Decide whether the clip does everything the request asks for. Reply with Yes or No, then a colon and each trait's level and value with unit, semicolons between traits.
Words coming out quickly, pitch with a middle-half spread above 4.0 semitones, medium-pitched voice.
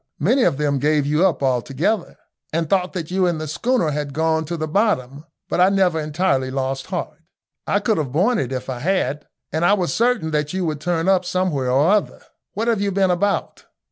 Yes: fast, 215 wpm; average, 4.6 semitones; medium, 160 Hz